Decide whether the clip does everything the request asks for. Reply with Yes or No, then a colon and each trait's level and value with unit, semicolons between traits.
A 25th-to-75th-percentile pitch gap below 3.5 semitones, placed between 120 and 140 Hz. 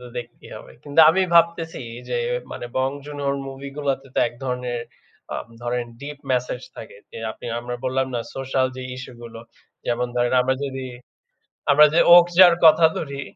Yes: average, 3.1 semitones; low, 135 Hz